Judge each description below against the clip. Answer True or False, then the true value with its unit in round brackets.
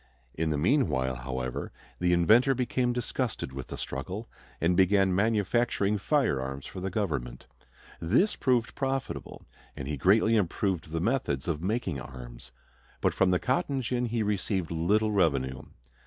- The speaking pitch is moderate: False (95 Hz)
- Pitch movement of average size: False (7.8 semitones)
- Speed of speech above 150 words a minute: False (145 wpm)